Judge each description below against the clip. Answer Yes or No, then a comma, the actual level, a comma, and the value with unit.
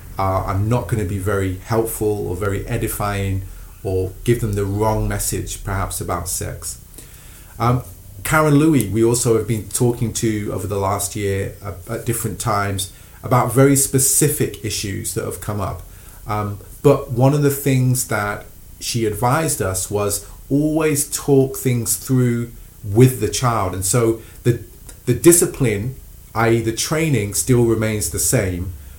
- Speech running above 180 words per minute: No, average, 155 wpm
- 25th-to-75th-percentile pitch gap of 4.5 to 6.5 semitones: No, average, 3.6 semitones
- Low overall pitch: Yes, low, 110 Hz